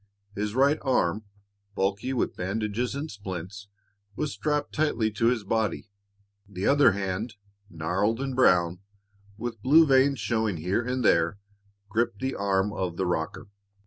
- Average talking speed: Yes, average, 145 wpm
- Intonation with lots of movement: No, average, 5.0 semitones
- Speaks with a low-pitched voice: Yes, low, 105 Hz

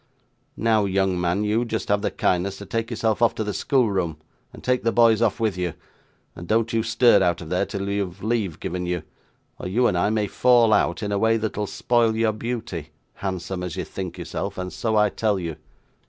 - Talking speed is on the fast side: Yes, fast, 220 wpm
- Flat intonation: No, average, 3.6 semitones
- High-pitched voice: No, low, 105 Hz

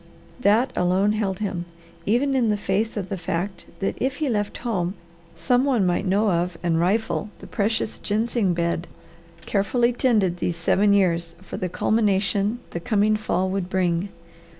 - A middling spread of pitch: Yes, average, 3.5 semitones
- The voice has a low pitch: No, high, 200 Hz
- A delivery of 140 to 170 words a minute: Yes, average, 165 wpm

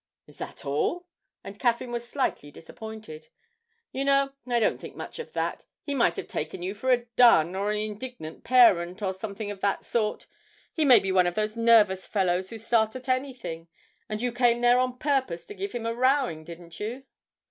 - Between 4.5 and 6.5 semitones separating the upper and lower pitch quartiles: Yes, average, 4.9 semitones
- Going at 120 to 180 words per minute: No, average, 200 wpm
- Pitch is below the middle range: No, high, 220 Hz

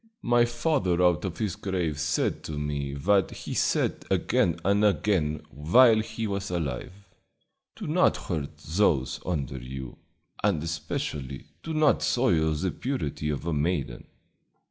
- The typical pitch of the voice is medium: No, very low, 85 Hz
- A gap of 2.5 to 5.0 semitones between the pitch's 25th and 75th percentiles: No, wide, 5.5 semitones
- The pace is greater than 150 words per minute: No, average, 145 wpm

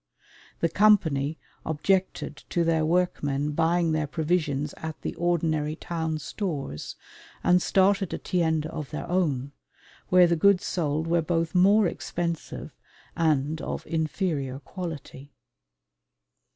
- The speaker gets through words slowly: Yes, slow, 120 wpm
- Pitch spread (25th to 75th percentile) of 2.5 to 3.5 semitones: Yes, average, 2.8 semitones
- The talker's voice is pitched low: No, medium, 160 Hz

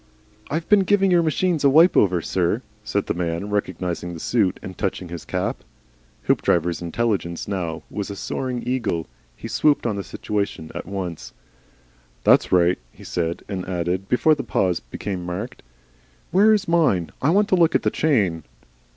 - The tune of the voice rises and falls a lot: Yes, wide, 8.4 semitones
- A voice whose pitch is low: Yes, low, 100 Hz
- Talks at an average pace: Yes, average, 170 wpm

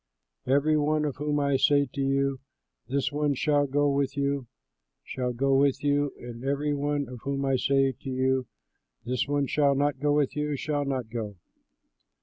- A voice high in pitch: No, medium, 140 Hz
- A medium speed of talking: Yes, average, 180 wpm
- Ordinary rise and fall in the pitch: No, narrow, 1.6 semitones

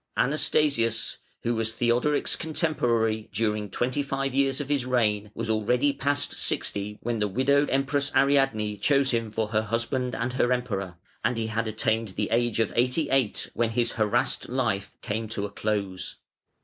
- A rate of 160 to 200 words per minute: Yes, average, 165 wpm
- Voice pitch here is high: No, low, 115 Hz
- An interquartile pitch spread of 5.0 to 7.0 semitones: No, average, 3.8 semitones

